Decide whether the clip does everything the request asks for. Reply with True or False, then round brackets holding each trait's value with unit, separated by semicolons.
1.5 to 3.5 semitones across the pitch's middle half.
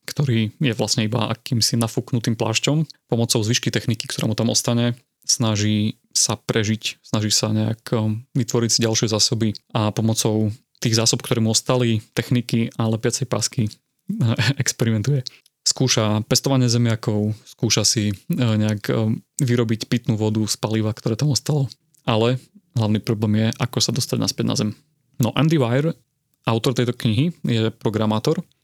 True (2.8 semitones)